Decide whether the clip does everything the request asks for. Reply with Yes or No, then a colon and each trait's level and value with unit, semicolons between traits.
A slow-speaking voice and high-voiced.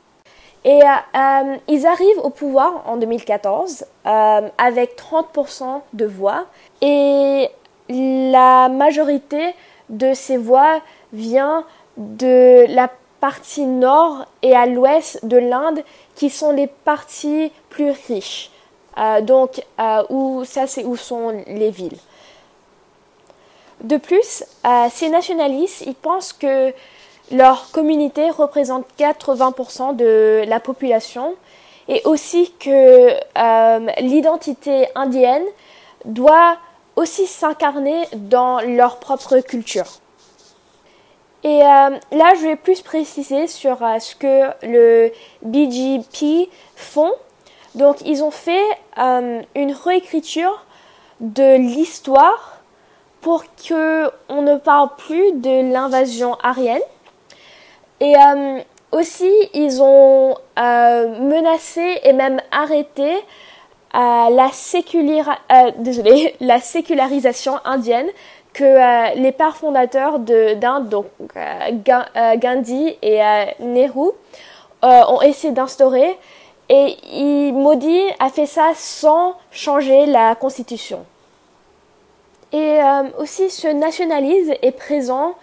Yes: slow, 110 wpm; very high, 275 Hz